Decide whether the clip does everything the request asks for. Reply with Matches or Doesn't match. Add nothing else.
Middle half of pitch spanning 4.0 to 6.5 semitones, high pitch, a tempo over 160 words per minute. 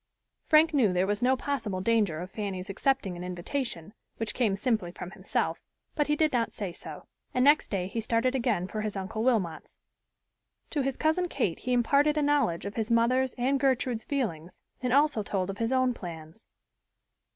Matches